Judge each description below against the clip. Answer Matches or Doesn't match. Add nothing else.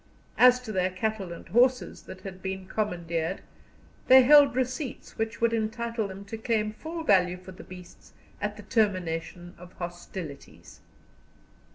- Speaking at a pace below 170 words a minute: Matches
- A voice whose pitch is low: Doesn't match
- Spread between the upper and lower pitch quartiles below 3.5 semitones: Doesn't match